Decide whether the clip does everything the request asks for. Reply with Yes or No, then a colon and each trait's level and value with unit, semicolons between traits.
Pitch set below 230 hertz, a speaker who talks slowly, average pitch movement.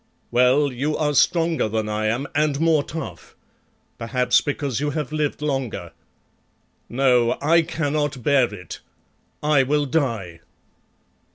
Yes: medium, 140 Hz; slow, 125 wpm; average, 3.8 semitones